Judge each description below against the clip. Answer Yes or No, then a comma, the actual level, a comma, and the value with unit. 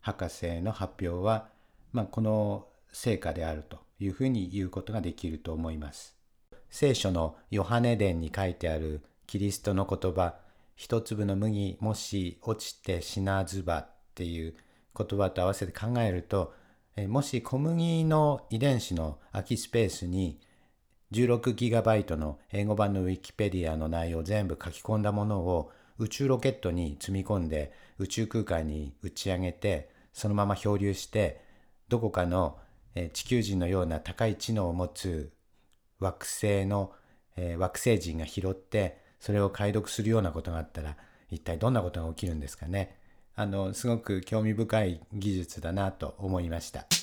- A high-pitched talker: No, very low, 95 Hz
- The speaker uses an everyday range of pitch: Yes, average, 4.0 semitones